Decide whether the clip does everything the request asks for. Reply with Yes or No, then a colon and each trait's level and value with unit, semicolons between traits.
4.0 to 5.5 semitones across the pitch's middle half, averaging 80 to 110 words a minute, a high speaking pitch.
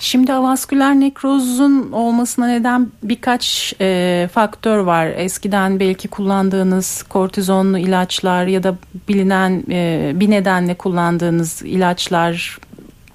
Yes: average, 4.7 semitones; average, 100 wpm; high, 195 Hz